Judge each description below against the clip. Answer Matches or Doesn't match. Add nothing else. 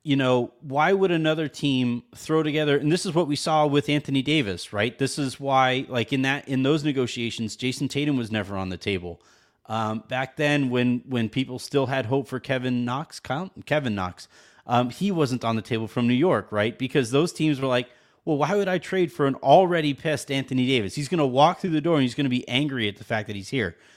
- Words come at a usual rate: Doesn't match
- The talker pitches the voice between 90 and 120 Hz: Doesn't match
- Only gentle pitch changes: Doesn't match